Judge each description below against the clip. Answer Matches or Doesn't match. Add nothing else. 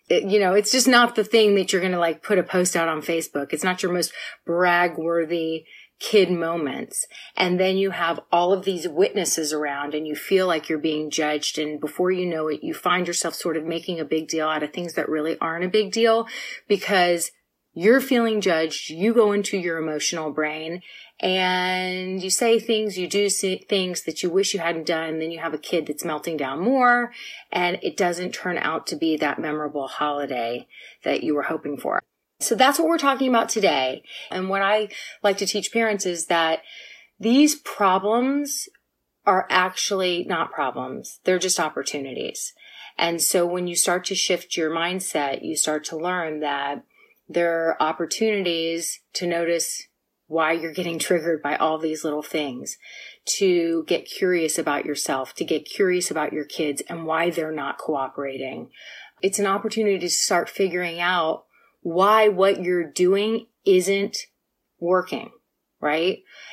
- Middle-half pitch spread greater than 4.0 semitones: Doesn't match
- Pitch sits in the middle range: Matches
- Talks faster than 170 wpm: Matches